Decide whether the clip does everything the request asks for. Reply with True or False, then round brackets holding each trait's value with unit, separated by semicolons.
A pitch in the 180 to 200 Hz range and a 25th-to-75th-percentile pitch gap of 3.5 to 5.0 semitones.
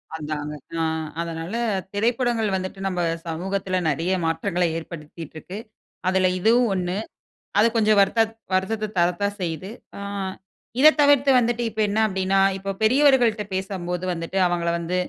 True (190 Hz; 3.9 semitones)